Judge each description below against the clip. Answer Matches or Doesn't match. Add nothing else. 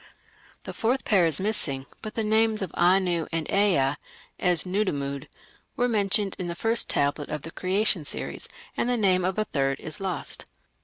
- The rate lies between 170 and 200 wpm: Matches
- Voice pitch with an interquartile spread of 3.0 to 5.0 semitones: Doesn't match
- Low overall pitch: Doesn't match